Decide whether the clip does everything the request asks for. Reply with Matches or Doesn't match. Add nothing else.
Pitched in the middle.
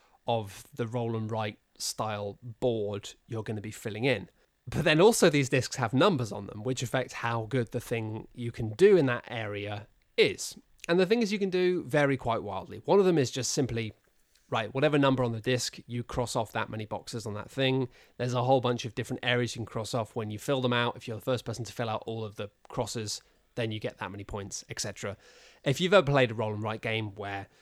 Doesn't match